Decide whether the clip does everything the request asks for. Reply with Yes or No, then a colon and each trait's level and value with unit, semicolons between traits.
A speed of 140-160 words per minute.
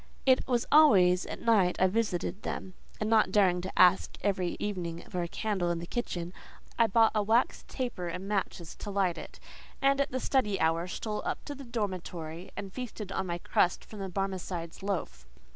No: average, 195 wpm